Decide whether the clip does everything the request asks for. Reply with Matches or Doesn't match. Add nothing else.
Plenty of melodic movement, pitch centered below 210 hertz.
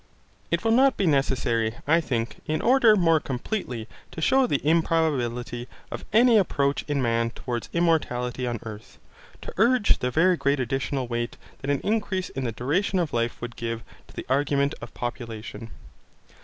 Matches